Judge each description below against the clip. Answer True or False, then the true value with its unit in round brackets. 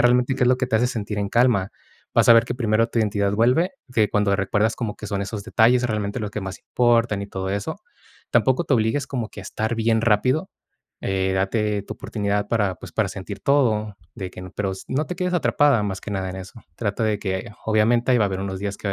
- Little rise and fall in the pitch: False (3.3 semitones)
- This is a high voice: False (110 Hz)